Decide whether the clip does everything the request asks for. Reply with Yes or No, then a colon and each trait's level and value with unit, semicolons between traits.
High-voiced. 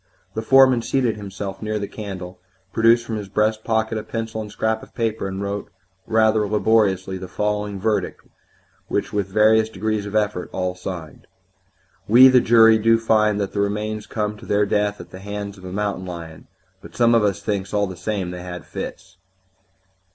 No: low, 105 Hz